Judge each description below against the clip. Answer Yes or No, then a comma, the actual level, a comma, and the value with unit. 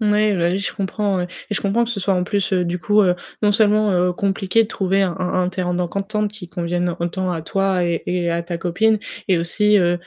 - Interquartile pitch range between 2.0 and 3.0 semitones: Yes, average, 2.7 semitones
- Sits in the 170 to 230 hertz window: Yes, high, 190 Hz